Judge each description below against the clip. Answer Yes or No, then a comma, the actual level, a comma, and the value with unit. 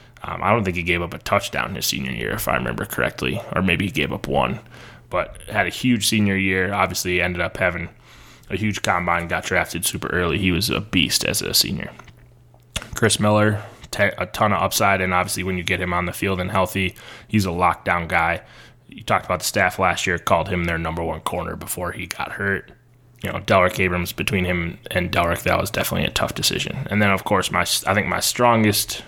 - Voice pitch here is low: Yes, very low, 95 Hz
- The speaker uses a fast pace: Yes, fast, 225 wpm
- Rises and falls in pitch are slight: No, average, 3.1 semitones